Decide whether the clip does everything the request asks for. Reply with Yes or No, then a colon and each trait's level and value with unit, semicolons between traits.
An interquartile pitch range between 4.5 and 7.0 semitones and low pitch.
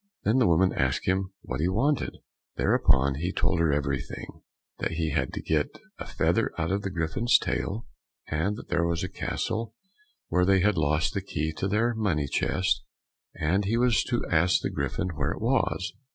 Yes: average, 4.9 semitones; very low, 90 Hz